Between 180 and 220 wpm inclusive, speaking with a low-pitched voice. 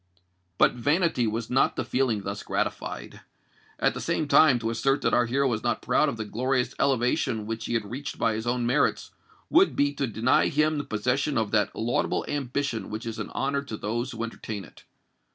Yes: fast, 205 wpm; low, 120 Hz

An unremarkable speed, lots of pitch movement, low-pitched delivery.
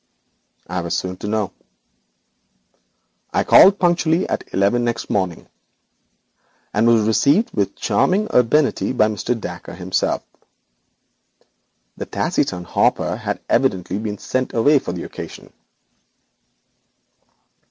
No: slow, 110 wpm; wide, 6.1 semitones; low, 110 Hz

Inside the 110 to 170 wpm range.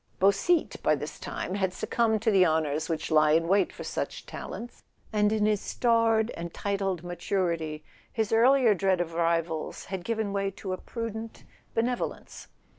Yes: average, 165 wpm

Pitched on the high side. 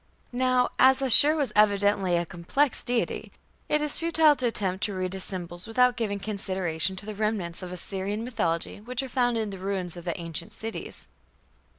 Yes: high, 205 Hz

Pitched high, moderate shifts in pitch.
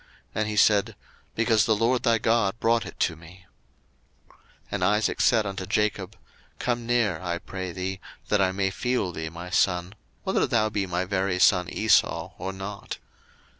No: low, 100 Hz; average, 3.2 semitones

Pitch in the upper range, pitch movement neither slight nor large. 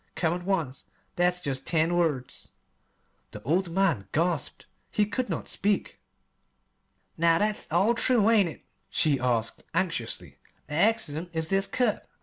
No: medium, 175 Hz; average, 4.0 semitones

